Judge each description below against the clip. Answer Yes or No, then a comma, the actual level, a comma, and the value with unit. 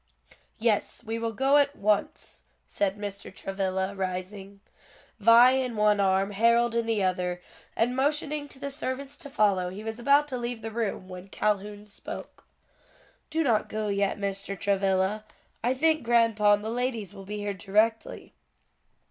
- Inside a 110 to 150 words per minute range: No, average, 160 wpm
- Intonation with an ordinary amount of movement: Yes, average, 3.4 semitones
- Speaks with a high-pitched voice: Yes, high, 215 Hz